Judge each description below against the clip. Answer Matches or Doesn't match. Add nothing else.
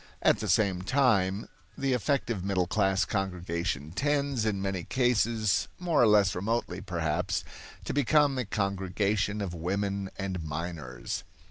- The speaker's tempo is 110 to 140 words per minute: Matches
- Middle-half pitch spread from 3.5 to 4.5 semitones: Matches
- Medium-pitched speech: Doesn't match